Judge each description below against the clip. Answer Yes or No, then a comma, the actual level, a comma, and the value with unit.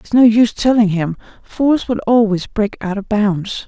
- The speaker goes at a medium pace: Yes, average, 195 wpm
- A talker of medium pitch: No, high, 215 Hz